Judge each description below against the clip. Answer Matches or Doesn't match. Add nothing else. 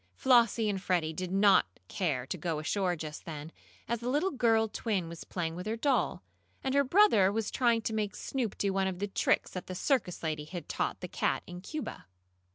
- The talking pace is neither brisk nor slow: Doesn't match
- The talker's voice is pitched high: Matches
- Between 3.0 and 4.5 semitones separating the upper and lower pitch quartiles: Doesn't match